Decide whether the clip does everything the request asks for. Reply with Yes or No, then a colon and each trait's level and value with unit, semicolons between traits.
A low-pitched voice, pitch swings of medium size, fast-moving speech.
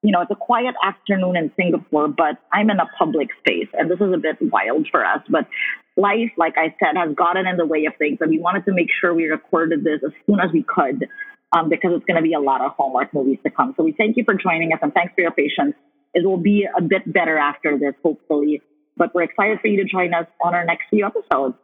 No: medium, 175 Hz; average, 3.8 semitones; fast, 265 wpm